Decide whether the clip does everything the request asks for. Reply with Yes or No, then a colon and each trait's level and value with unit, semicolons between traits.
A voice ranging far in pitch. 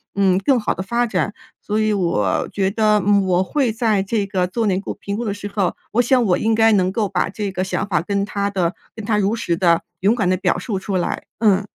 No: narrow, 2.6 semitones